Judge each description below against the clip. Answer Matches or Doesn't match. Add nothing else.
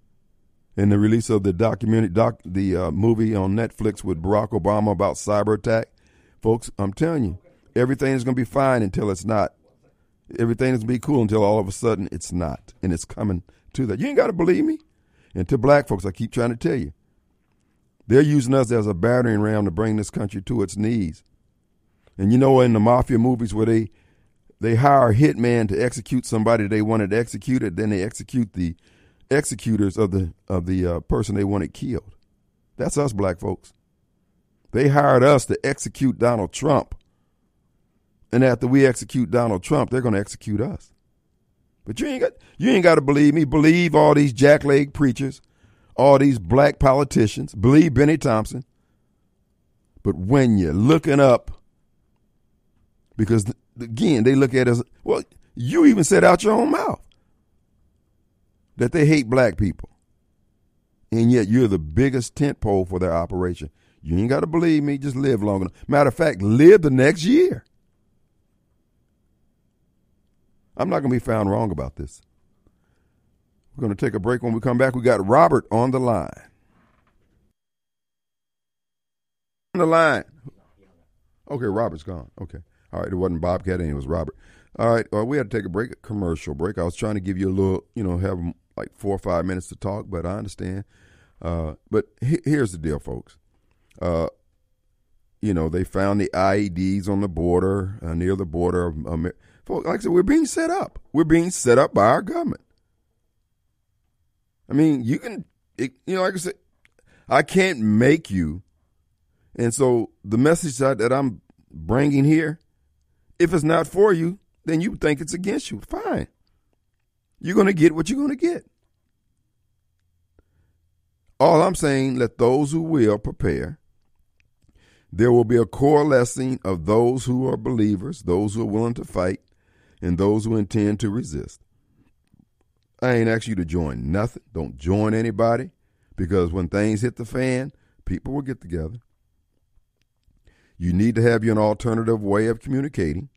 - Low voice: Matches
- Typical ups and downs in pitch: Doesn't match